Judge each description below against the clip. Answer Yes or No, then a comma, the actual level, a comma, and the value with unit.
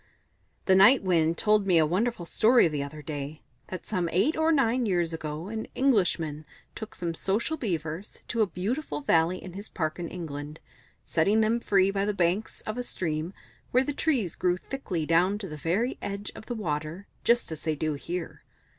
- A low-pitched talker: No, medium, 185 Hz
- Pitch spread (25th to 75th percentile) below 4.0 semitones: No, average, 5.2 semitones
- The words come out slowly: No, average, 190 wpm